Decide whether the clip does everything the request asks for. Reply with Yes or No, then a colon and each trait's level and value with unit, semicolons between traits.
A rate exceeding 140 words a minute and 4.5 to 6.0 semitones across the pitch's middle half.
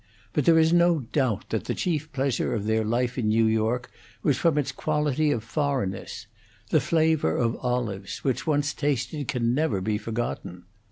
Yes: average, 175 wpm; average, 5.1 semitones